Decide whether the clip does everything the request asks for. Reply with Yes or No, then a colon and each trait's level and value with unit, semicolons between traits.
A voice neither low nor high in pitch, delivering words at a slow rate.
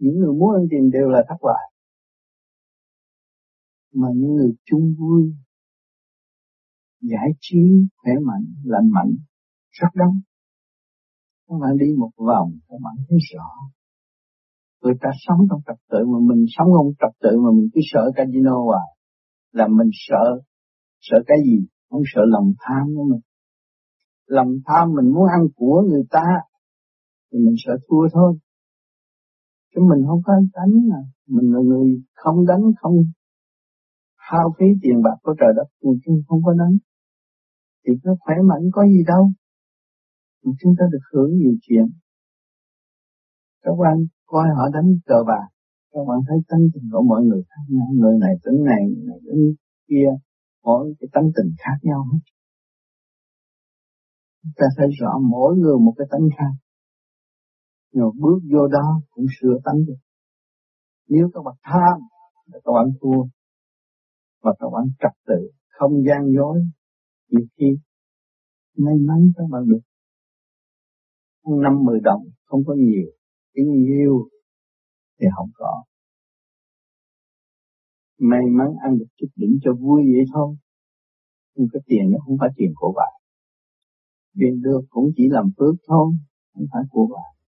Yes: medium, 150 Hz; slow, 155 wpm